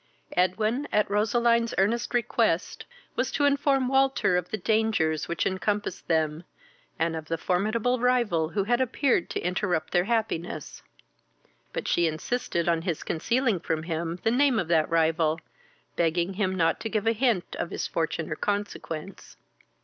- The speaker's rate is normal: Yes, average, 155 wpm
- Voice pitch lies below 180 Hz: No, high, 195 Hz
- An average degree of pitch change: No, wide, 5.9 semitones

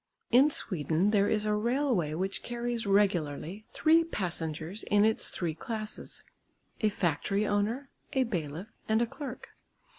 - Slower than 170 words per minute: Yes, average, 140 wpm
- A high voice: Yes, high, 210 Hz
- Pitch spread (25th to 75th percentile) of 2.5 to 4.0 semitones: No, average, 5.1 semitones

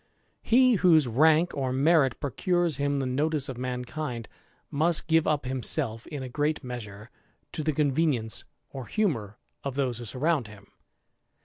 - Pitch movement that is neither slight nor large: Yes, average, 4.1 semitones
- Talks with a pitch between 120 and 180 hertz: Yes, medium, 140 Hz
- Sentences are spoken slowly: No, average, 150 wpm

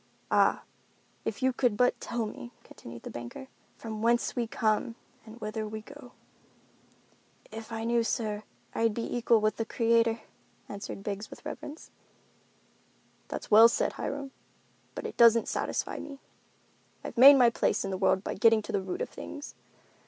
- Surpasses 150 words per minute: Yes, average, 165 wpm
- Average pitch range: No, narrow, 2.1 semitones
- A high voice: Yes, high, 230 Hz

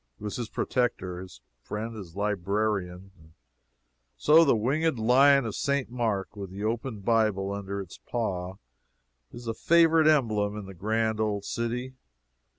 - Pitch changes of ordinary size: Yes, average, 3.7 semitones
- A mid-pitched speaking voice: No, low, 110 Hz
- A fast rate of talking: No, average, 155 wpm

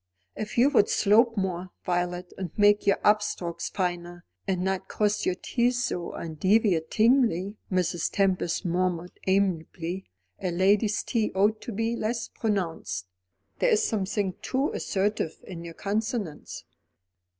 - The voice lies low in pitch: No, high, 195 Hz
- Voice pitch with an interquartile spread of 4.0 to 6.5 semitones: No, average, 3.4 semitones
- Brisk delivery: No, slow, 135 wpm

